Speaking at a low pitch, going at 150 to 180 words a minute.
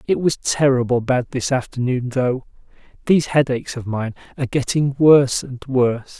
Yes: low, 130 Hz; average, 155 wpm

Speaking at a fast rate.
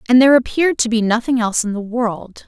Yes: fast, 245 wpm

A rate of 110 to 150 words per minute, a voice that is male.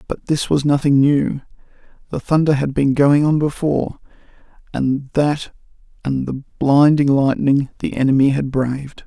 Yes: average, 145 wpm; male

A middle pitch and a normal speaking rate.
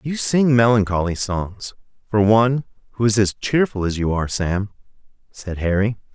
No: low, 105 Hz; average, 155 wpm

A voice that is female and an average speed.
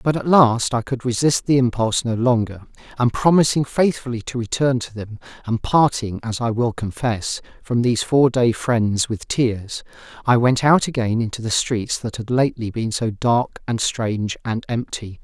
No: male; average, 185 wpm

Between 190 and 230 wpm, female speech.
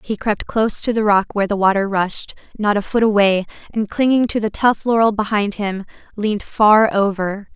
Yes: average, 200 wpm; female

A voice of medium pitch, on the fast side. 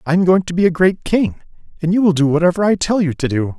Yes: medium, 175 Hz; fast, 300 wpm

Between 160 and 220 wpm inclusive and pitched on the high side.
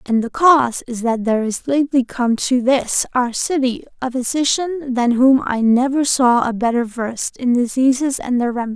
Yes: average, 190 wpm; very high, 255 Hz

